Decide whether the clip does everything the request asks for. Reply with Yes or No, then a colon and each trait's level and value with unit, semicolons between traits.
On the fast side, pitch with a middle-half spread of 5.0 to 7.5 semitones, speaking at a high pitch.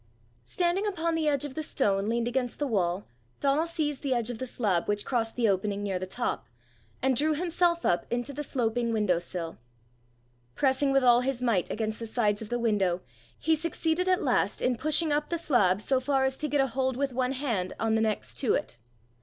Yes: fast, 215 wpm; average, 5.3 semitones; very high, 250 Hz